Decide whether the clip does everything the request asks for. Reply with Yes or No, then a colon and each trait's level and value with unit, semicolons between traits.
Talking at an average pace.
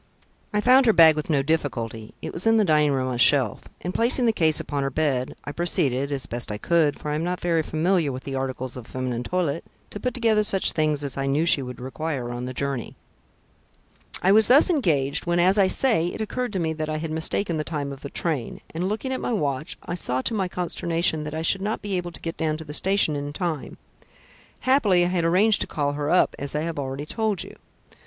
No: fast, 245 wpm